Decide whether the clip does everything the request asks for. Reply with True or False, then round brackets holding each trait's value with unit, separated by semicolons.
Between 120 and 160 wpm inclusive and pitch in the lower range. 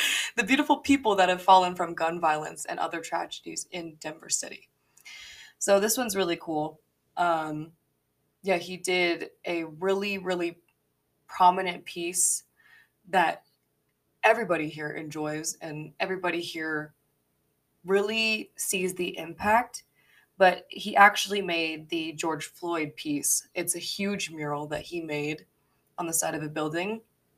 False (135 wpm; 175 Hz)